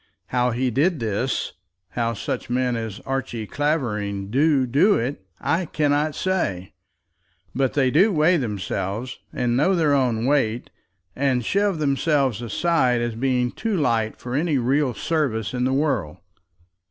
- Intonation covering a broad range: No, average, 4.3 semitones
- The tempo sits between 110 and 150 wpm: Yes, average, 145 wpm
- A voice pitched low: Yes, low, 130 Hz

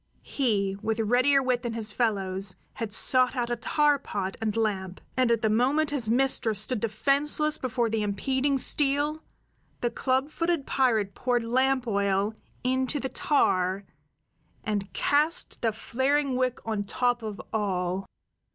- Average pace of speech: Yes, average, 150 wpm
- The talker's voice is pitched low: No, high, 240 Hz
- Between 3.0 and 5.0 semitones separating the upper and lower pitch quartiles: Yes, average, 4.2 semitones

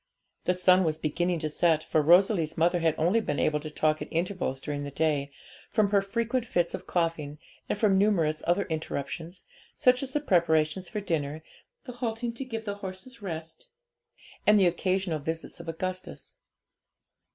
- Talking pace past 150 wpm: Yes, average, 175 wpm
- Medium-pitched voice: Yes, medium, 175 Hz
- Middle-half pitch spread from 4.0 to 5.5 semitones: Yes, average, 4.3 semitones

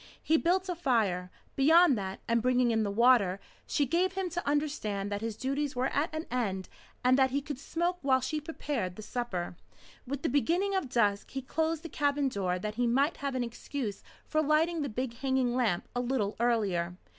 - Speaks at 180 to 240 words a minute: Yes, average, 200 wpm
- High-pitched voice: Yes, very high, 260 Hz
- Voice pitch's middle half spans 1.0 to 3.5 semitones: No, average, 5.3 semitones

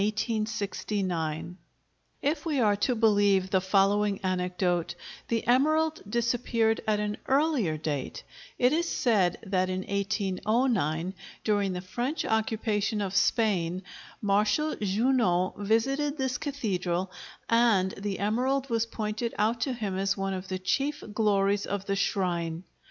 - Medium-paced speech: No, slow, 130 wpm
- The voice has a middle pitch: No, high, 205 Hz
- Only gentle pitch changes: No, average, 3.8 semitones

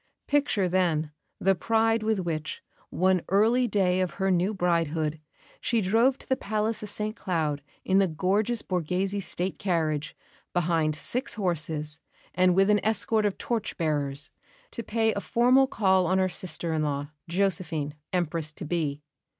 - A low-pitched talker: No, medium, 185 Hz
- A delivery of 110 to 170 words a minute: Yes, average, 160 wpm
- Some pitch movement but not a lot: Yes, average, 4.7 semitones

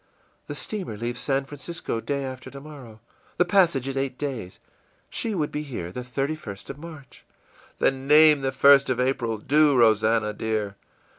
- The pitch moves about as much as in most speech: Yes, average, 4.1 semitones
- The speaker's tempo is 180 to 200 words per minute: No, average, 165 wpm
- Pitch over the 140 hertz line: No, low, 135 Hz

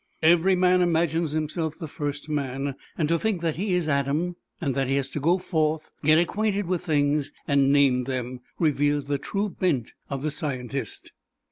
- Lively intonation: No, average, 3.6 semitones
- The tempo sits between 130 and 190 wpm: Yes, average, 180 wpm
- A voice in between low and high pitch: Yes, medium, 155 Hz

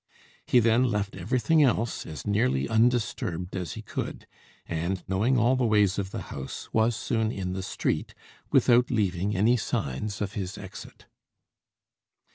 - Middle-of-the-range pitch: No, low, 105 Hz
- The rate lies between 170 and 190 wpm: No, average, 150 wpm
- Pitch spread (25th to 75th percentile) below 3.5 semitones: No, average, 4.1 semitones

